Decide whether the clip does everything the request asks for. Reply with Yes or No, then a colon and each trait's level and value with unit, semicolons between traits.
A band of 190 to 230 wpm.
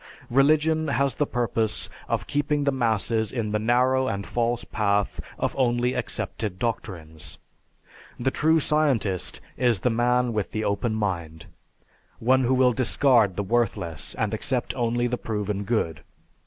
No: average, 145 wpm